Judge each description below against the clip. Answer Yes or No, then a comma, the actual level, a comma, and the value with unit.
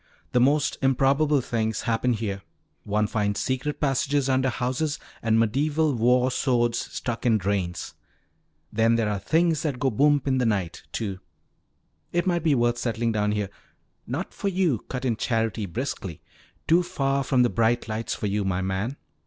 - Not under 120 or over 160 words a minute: No, average, 170 wpm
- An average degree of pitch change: Yes, average, 4.2 semitones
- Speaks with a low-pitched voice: Yes, low, 120 Hz